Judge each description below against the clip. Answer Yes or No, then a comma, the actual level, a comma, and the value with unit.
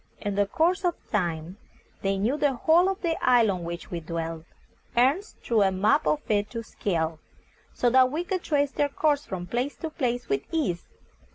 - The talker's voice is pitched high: Yes, high, 235 Hz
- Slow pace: No, average, 195 wpm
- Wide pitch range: Yes, wide, 8.0 semitones